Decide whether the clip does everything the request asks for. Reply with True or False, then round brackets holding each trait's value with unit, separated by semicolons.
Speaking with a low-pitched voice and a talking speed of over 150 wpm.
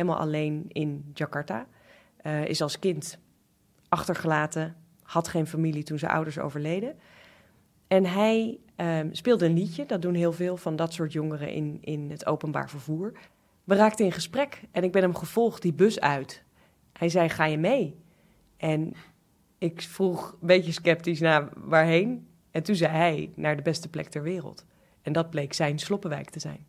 False (165 Hz; 175 wpm)